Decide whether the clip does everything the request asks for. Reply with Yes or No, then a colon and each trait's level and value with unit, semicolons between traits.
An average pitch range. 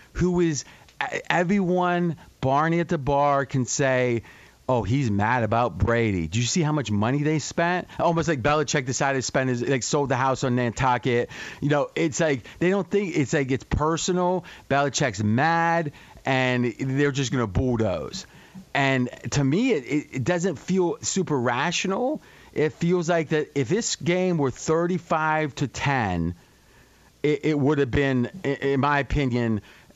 Yes: average, 4.7 semitones